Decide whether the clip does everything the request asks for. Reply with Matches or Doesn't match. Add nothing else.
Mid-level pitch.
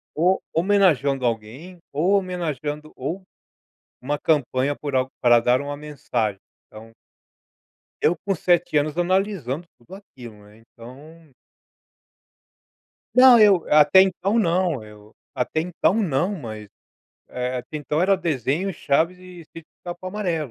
Matches